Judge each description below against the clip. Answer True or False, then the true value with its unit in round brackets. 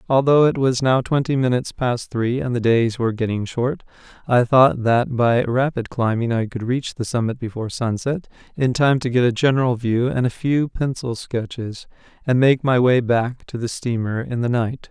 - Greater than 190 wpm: True (200 wpm)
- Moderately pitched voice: False (125 Hz)